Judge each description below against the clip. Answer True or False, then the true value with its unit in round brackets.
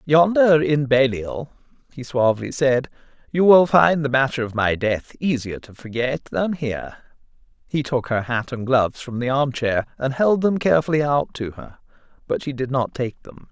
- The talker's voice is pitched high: False (135 Hz)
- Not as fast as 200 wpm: True (185 wpm)